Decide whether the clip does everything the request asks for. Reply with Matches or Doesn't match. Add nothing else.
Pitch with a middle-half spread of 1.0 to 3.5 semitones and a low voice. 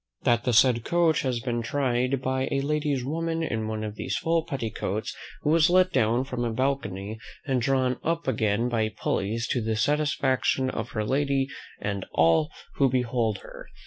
Doesn't match